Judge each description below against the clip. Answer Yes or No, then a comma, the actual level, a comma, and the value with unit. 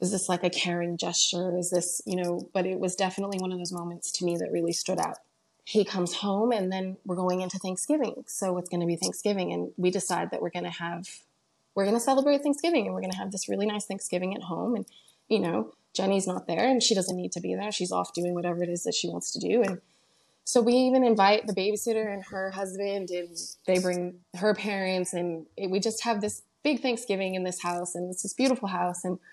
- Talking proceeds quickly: Yes, fast, 245 wpm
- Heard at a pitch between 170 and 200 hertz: Yes, medium, 185 Hz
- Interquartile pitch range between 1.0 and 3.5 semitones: Yes, average, 2.8 semitones